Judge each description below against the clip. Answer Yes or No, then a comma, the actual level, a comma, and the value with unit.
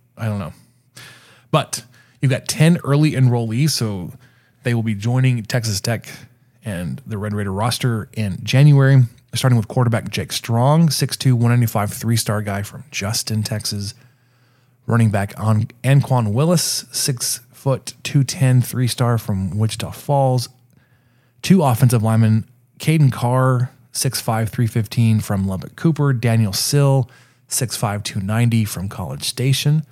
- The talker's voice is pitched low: Yes, low, 125 Hz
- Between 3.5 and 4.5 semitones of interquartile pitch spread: No, average, 2.9 semitones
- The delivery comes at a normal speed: No, slow, 130 wpm